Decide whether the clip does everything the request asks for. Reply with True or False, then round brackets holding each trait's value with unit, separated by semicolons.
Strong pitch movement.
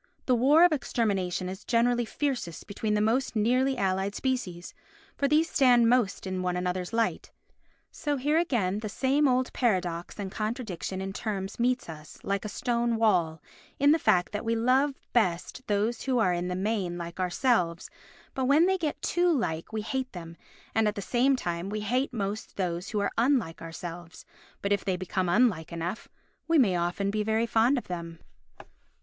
True (5.7 semitones)